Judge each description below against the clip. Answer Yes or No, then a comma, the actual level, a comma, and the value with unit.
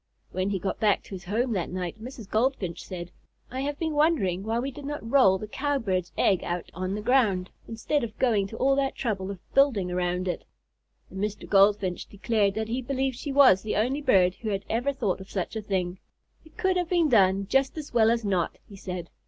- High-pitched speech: Yes, high, 215 Hz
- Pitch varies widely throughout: Yes, wide, 5.8 semitones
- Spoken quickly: Yes, fast, 220 wpm